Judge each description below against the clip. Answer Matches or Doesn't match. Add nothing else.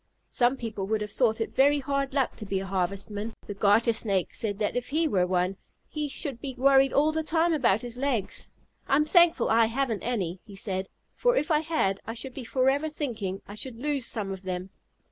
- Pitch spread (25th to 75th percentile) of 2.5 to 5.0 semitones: Doesn't match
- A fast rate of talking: Matches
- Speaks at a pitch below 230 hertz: Doesn't match